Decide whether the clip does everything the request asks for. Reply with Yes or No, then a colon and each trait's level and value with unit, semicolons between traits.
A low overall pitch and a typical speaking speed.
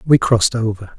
Yes: low, 115 Hz; average, 185 wpm